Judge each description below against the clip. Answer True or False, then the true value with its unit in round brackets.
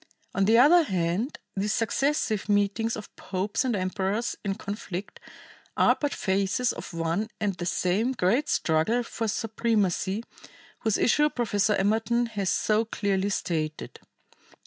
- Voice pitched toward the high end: True (210 Hz)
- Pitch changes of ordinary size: True (3.2 semitones)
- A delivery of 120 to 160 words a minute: True (135 wpm)